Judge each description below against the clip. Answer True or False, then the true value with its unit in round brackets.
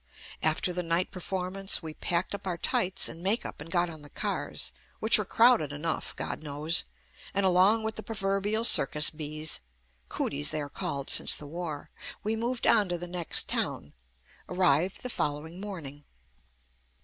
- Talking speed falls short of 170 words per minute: False (175 wpm)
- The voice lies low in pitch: False (175 Hz)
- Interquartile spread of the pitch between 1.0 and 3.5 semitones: False (4.3 semitones)